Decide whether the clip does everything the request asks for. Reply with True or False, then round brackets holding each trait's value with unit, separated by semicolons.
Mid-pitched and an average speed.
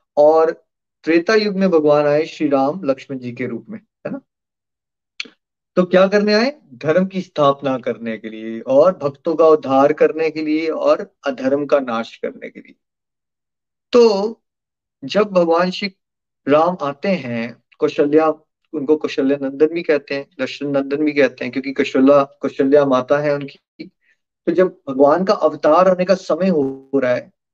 True (150 Hz; 165 wpm)